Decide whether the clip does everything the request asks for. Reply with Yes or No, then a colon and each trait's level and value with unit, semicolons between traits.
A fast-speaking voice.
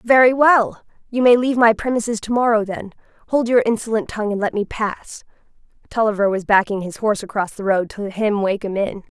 No: average, 195 wpm